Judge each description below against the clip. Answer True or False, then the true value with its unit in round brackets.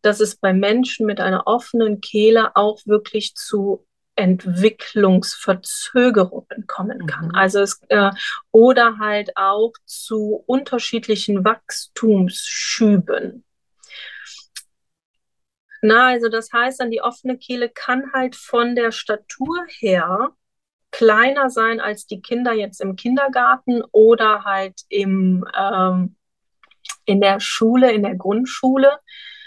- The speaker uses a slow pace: True (110 wpm)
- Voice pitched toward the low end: False (220 Hz)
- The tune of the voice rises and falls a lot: False (3.8 semitones)